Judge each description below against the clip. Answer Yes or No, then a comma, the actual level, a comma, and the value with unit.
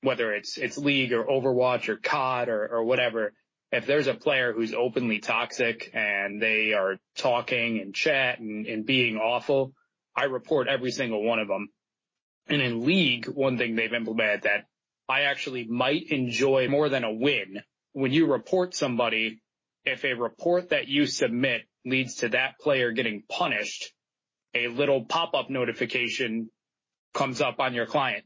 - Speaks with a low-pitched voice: Yes, low, 125 Hz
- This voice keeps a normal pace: Yes, average, 160 wpm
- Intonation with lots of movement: No, average, 3.1 semitones